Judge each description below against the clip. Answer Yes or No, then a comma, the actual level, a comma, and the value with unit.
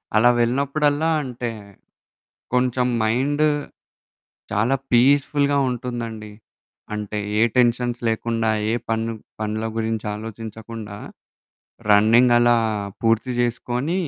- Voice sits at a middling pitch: No, low, 120 Hz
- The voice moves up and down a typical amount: No, narrow, 2.2 semitones